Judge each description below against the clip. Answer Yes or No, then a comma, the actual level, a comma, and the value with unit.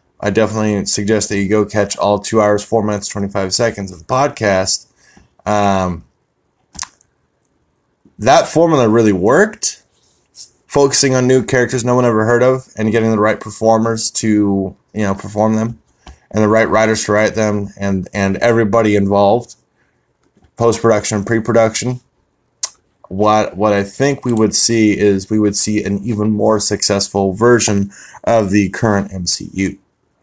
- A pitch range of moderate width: No, narrow, 2.3 semitones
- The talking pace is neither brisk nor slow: Yes, average, 150 wpm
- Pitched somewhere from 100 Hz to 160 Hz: Yes, low, 105 Hz